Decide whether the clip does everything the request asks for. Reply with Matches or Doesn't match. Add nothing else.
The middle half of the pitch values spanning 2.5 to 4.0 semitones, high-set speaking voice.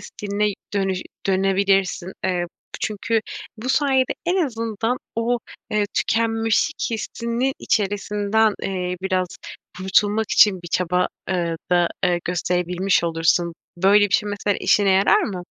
Matches